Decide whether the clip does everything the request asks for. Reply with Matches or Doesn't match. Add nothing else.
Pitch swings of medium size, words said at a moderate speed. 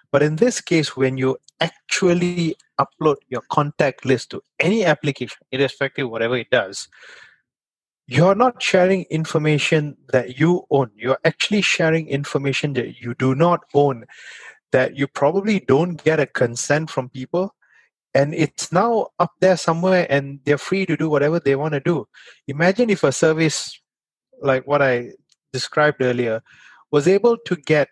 Matches